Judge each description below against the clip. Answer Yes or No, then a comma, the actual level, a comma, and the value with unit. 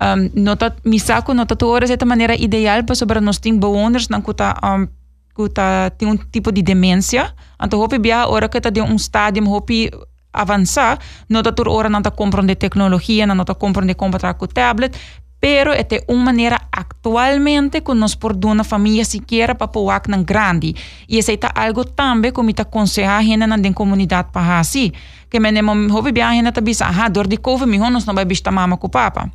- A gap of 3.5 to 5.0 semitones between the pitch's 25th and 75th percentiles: No, average, 2.9 semitones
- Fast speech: No, average, 190 wpm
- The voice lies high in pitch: Yes, high, 215 Hz